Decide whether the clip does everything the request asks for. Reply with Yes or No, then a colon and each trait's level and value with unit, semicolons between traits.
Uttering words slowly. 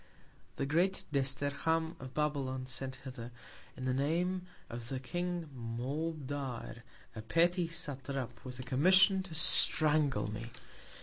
Yes: slow, 125 wpm